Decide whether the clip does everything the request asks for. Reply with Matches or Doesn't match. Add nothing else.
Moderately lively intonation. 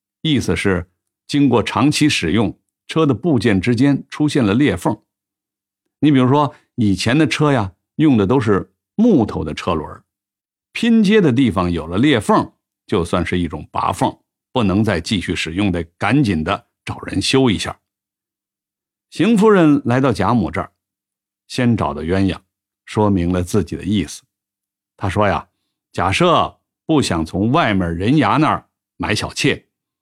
Doesn't match